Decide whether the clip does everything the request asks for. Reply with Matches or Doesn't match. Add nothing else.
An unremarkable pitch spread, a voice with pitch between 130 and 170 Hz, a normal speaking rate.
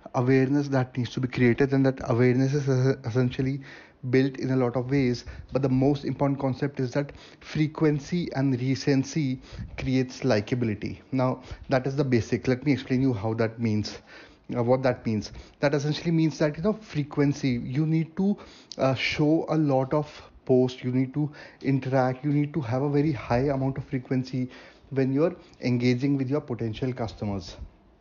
Doesn't match